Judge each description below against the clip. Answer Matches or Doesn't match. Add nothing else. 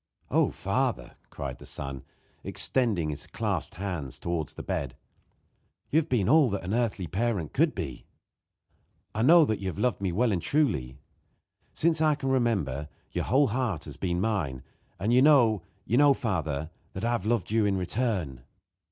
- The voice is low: Matches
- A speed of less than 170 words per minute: Doesn't match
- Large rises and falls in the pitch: Matches